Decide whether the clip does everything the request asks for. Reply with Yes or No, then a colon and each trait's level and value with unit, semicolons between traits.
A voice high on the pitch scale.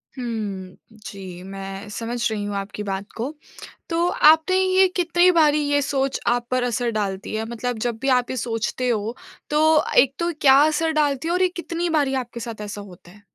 Yes: high, 240 Hz